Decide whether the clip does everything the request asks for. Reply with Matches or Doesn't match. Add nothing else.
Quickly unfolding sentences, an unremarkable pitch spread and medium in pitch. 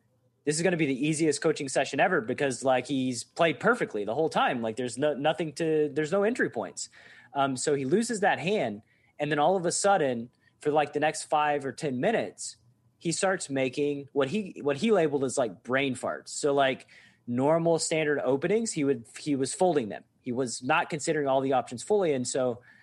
Matches